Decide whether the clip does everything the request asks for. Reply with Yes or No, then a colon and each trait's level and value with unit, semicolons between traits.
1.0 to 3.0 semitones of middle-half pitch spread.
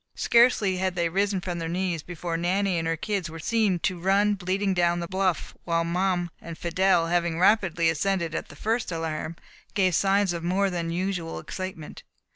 Yes: narrow, 2.5 semitones